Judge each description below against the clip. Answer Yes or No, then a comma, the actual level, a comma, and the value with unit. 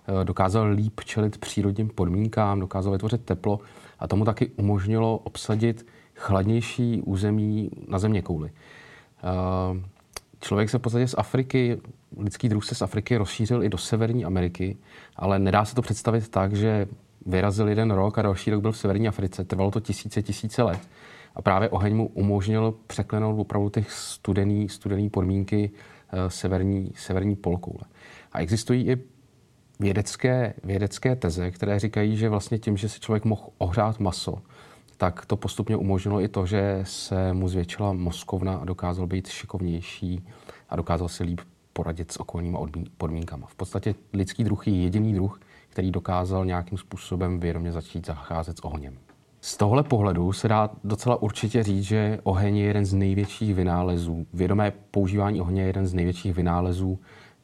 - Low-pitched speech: Yes, low, 100 Hz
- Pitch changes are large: No, average, 2.7 semitones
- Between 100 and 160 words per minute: Yes, average, 155 wpm